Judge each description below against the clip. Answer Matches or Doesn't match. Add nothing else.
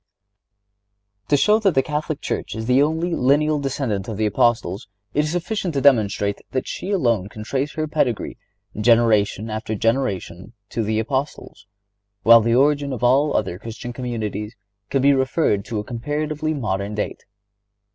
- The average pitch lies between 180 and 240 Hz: Doesn't match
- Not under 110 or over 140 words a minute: Doesn't match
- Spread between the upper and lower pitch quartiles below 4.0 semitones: Doesn't match